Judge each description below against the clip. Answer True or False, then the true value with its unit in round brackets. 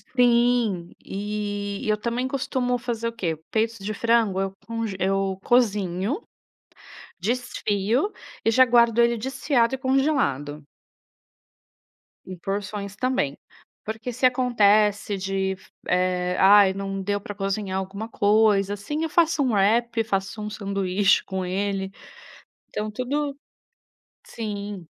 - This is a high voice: True (210 Hz)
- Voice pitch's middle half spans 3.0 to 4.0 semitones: True (3.4 semitones)